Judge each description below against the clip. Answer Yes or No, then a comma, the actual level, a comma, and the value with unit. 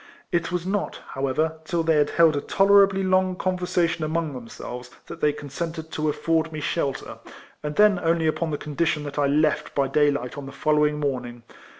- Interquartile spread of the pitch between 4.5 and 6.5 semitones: No, average, 2.8 semitones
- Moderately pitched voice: Yes, medium, 155 Hz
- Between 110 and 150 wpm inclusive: No, average, 195 wpm